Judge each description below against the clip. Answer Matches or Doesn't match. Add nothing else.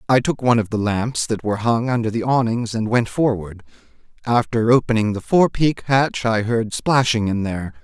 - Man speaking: Matches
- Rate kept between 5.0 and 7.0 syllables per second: Matches